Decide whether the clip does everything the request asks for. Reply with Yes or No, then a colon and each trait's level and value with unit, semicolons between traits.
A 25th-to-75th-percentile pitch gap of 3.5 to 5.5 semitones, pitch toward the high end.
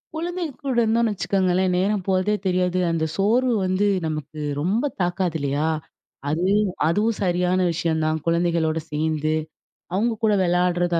No: average, 4.2 semitones; medium, 180 Hz